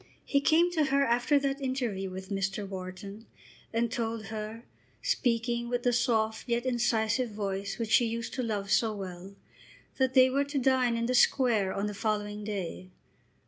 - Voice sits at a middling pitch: No, high, 230 Hz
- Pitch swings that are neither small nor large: Yes, average, 3.6 semitones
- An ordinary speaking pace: Yes, average, 175 wpm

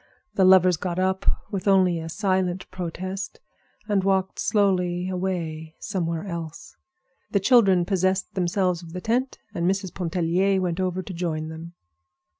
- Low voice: No, medium, 185 Hz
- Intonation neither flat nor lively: No, narrow, 1.9 semitones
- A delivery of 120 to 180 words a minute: Yes, average, 145 wpm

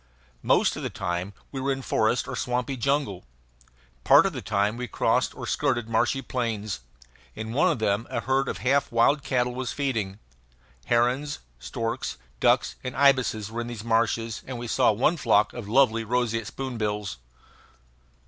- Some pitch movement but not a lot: Yes, average, 3.2 semitones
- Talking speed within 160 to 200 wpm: Yes, average, 165 wpm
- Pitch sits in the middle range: No, low, 120 Hz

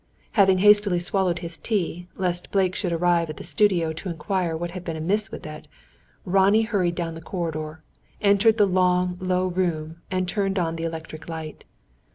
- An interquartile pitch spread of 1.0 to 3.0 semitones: Yes, average, 2.7 semitones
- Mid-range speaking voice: Yes, medium, 180 Hz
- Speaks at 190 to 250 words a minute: No, average, 180 wpm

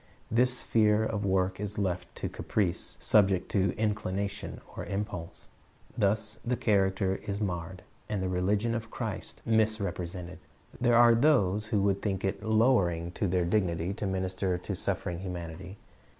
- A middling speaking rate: Yes, average, 150 wpm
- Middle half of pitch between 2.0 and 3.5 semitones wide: Yes, average, 2.8 semitones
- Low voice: Yes, low, 100 Hz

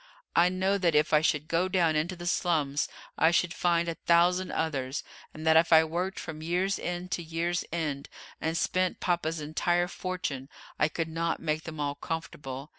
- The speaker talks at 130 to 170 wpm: No, average, 190 wpm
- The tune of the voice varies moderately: No, narrow, 2.2 semitones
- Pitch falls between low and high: Yes, medium, 165 Hz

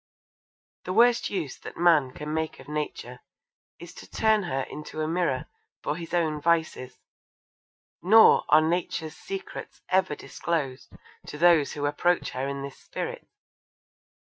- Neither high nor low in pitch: Yes, medium, 160 Hz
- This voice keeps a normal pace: Yes, average, 145 wpm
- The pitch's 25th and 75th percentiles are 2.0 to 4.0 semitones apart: Yes, average, 3.0 semitones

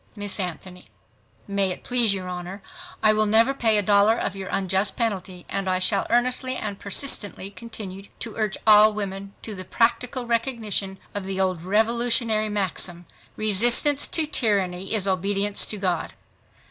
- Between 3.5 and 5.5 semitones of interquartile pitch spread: No, average, 2.9 semitones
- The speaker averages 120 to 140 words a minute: No, average, 155 wpm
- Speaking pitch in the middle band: No, high, 205 Hz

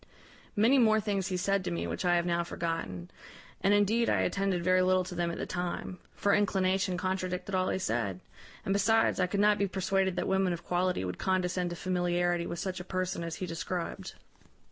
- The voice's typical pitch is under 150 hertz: No, medium, 185 Hz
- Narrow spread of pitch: Yes, narrow, 1.8 semitones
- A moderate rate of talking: No, fast, 210 wpm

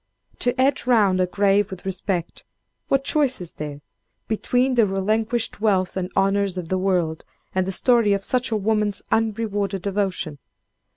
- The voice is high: Yes, high, 200 Hz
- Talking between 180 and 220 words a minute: No, average, 160 wpm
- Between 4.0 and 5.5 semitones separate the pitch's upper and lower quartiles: No, average, 3.1 semitones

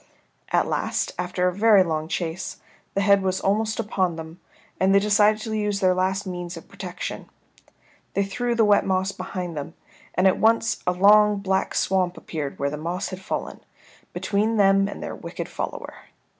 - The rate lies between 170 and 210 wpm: Yes, average, 180 wpm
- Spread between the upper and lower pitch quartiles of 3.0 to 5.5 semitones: No, narrow, 2.4 semitones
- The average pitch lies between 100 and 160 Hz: No, high, 190 Hz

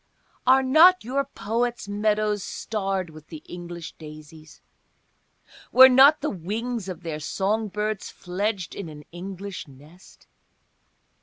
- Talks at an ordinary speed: No, slow, 125 wpm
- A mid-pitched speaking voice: No, high, 200 Hz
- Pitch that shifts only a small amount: No, average, 5.0 semitones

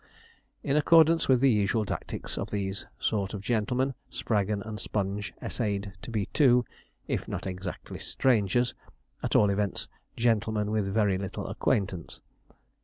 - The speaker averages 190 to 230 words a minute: No, average, 140 wpm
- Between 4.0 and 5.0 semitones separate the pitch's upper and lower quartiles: No, average, 3.5 semitones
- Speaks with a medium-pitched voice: No, low, 105 Hz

